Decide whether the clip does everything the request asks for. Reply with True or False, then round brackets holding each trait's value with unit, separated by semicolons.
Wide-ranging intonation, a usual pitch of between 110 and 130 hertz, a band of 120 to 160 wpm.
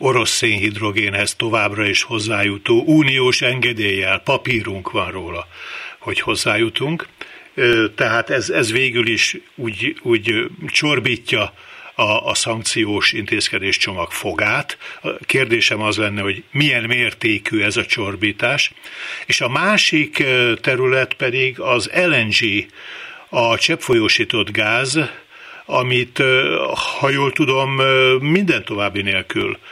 False (5.8 semitones; 125 Hz; 105 wpm)